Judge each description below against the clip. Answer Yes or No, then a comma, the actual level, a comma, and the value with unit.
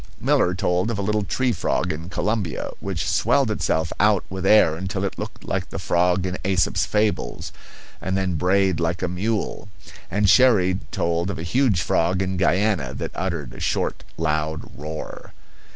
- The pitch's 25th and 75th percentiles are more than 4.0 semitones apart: No, average, 3.2 semitones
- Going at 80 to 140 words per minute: No, average, 170 wpm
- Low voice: Yes, very low, 95 Hz